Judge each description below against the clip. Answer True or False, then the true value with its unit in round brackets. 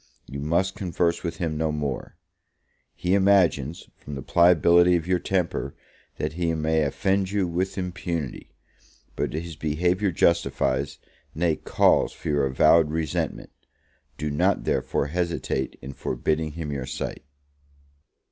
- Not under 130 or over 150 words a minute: True (135 wpm)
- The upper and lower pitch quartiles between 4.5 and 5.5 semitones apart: False (2.9 semitones)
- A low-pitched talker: True (80 Hz)